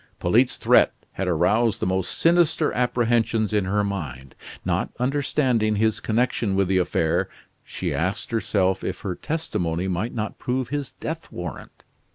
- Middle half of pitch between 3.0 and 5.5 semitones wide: Yes, average, 4.9 semitones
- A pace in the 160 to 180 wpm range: No, average, 150 wpm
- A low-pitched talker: Yes, low, 110 Hz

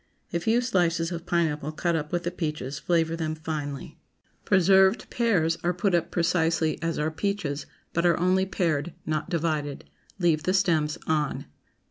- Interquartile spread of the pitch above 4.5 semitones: No, narrow, 2.5 semitones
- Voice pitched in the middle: Yes, medium, 165 Hz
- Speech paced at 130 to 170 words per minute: Yes, average, 160 wpm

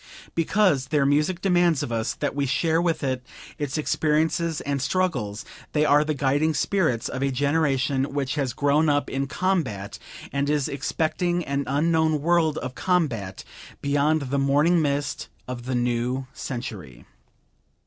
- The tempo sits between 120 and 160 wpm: Yes, average, 150 wpm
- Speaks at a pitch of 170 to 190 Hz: No, medium, 145 Hz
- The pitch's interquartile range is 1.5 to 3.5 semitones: Yes, average, 3.2 semitones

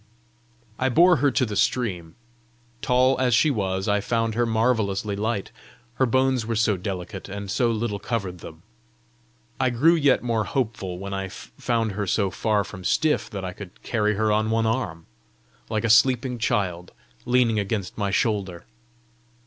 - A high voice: No, low, 110 Hz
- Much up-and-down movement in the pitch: No, average, 3.6 semitones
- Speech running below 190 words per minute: Yes, average, 165 wpm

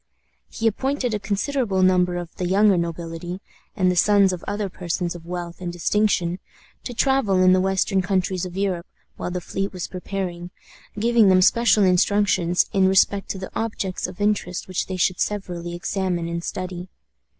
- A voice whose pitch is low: No, medium, 185 Hz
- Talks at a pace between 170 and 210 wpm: Yes, average, 175 wpm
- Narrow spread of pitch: Yes, narrow, 2.3 semitones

